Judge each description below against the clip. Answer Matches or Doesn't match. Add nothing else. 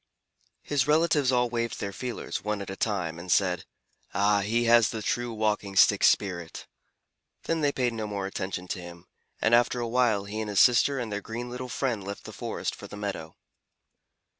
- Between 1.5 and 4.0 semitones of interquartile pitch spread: Matches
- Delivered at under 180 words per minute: Doesn't match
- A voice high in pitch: Doesn't match